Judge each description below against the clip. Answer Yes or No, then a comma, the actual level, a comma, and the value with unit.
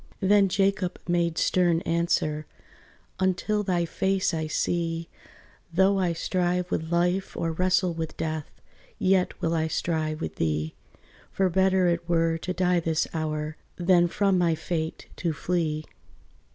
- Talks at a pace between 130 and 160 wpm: Yes, average, 140 wpm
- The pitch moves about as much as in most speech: No, narrow, 2.3 semitones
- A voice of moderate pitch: Yes, medium, 175 Hz